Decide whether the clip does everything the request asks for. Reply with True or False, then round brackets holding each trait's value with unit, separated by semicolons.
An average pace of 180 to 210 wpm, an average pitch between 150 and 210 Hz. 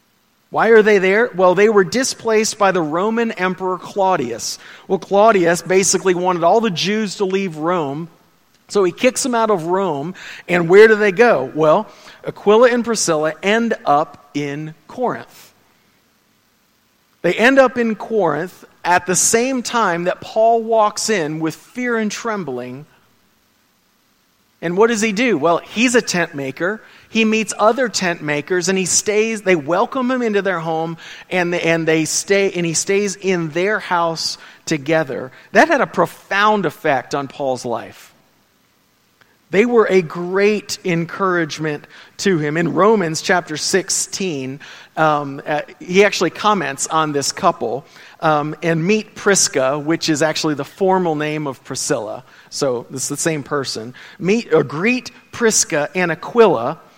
False (155 wpm; 185 Hz)